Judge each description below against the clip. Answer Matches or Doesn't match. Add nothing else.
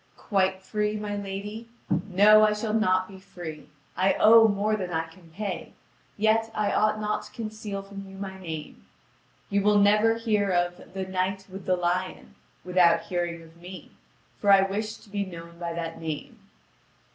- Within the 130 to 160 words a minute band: Doesn't match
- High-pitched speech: Matches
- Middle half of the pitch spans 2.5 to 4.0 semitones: Matches